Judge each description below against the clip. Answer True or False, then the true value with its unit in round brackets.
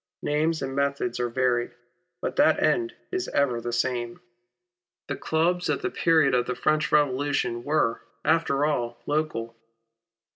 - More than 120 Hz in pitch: True (140 Hz)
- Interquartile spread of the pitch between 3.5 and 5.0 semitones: True (4.3 semitones)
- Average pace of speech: True (145 wpm)